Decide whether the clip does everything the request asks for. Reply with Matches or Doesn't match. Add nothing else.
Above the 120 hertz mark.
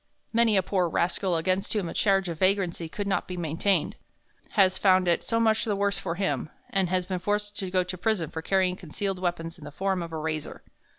Matches